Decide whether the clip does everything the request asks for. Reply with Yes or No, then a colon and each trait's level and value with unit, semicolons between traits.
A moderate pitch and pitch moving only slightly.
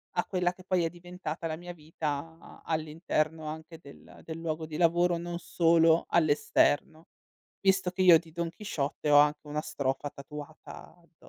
Yes: medium, 165 Hz; narrow, 2.2 semitones